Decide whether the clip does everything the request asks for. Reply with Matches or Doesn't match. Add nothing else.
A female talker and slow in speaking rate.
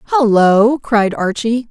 Matches